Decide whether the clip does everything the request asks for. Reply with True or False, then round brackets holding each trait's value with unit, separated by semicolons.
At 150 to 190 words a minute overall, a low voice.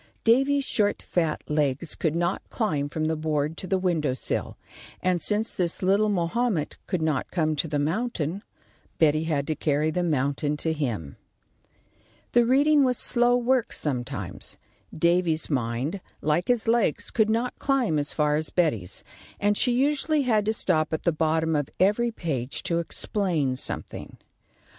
False (160 wpm; 170 Hz)